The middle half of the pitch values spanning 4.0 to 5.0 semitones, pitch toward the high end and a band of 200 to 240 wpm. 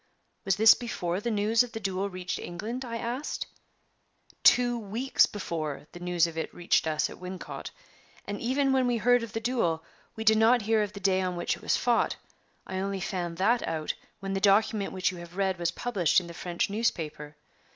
Yes: average, 4.6 semitones; high, 195 Hz; fast, 205 wpm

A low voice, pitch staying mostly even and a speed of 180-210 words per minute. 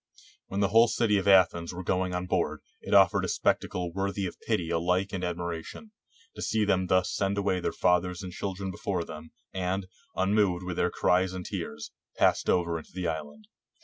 Yes: very low, 90 Hz; narrow, 1.9 semitones; average, 200 wpm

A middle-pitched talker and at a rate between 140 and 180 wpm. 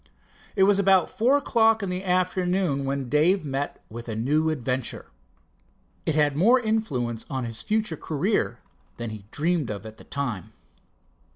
Yes: medium, 155 Hz; average, 160 wpm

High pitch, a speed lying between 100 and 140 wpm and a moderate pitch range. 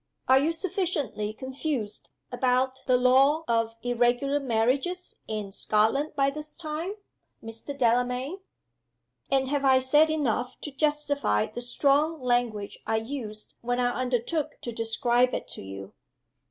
Yes: very high, 255 Hz; slow, 135 wpm; average, 3.8 semitones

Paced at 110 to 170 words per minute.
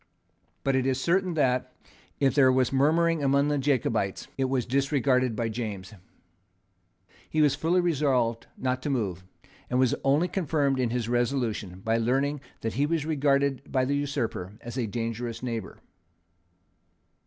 Yes: average, 155 wpm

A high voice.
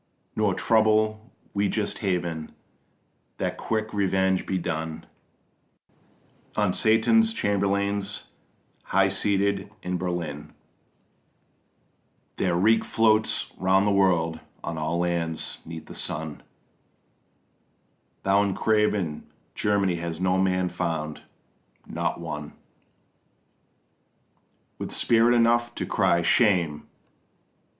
No: very low, 95 Hz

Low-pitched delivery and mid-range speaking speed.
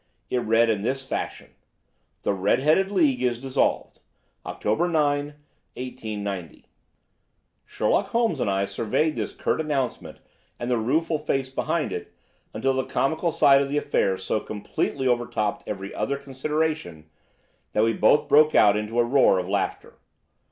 Yes: low, 130 Hz; average, 150 wpm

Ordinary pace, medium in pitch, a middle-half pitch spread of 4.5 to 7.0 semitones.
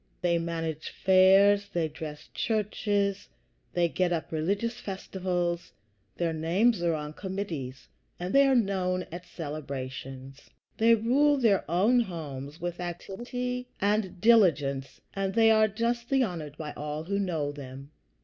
No: slow, 130 wpm; medium, 180 Hz; average, 5.0 semitones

